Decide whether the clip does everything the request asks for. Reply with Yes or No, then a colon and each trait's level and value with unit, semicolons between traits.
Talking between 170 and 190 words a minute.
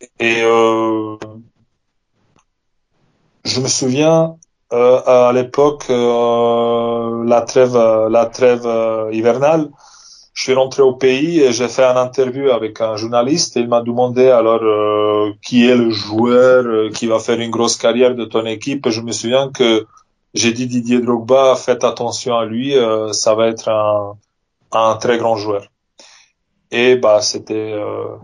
No: average, 155 wpm